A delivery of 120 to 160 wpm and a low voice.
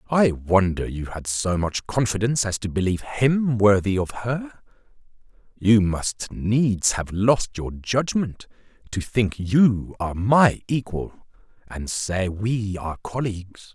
Yes: average, 140 wpm; low, 105 Hz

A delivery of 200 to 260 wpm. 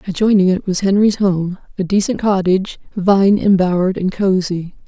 No: slow, 135 wpm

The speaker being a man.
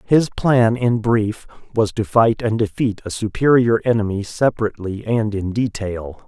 Yes: male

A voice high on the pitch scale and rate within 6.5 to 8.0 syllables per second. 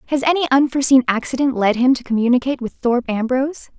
Yes: very high, 255 Hz; 7.0 syllables/s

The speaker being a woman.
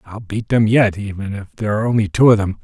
No: male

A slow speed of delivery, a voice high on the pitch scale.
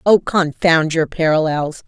No: slow, 130 wpm; medium, 165 Hz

